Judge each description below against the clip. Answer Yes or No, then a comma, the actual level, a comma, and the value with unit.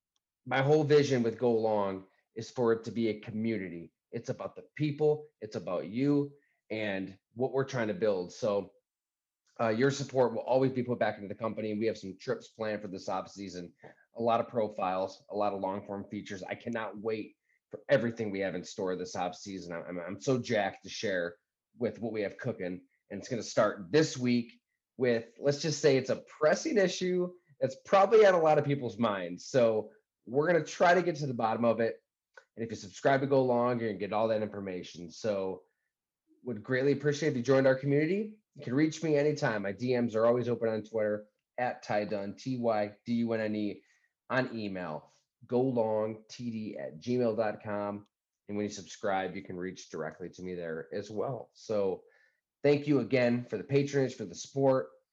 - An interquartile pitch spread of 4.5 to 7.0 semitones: Yes, average, 4.9 semitones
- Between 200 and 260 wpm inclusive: Yes, fast, 205 wpm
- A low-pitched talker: Yes, low, 115 Hz